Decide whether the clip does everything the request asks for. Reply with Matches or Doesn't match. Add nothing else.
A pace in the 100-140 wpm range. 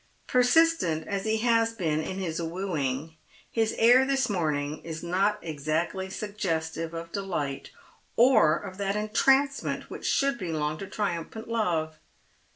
Matches